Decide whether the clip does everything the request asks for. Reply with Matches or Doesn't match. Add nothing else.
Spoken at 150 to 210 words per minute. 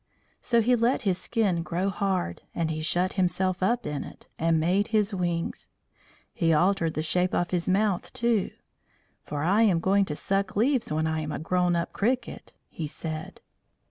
Matches